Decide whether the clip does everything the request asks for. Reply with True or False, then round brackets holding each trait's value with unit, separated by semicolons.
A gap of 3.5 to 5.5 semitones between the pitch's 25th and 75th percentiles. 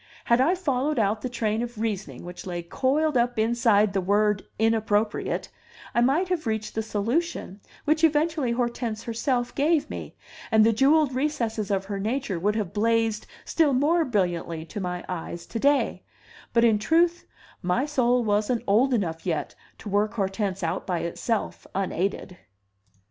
True (4.5 semitones)